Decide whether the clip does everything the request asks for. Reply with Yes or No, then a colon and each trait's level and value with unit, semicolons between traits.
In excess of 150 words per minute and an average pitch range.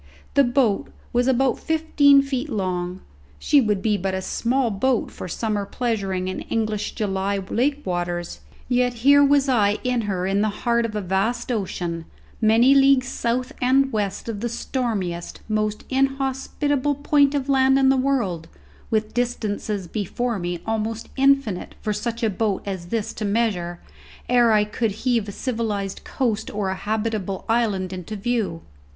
Yes: average, 160 wpm; average, 4.4 semitones